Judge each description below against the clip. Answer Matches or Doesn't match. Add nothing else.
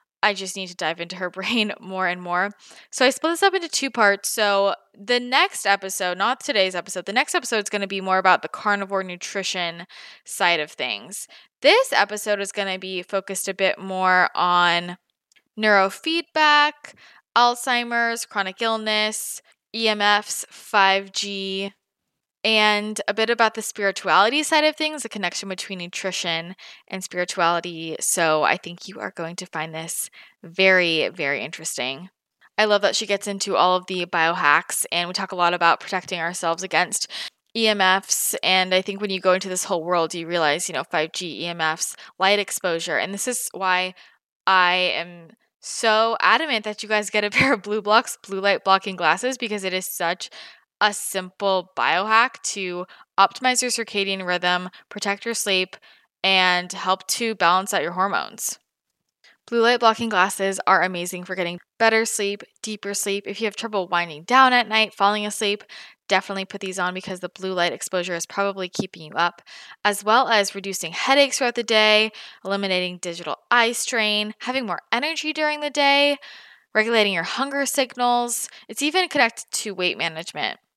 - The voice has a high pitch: Matches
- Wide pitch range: Doesn't match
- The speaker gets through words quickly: Doesn't match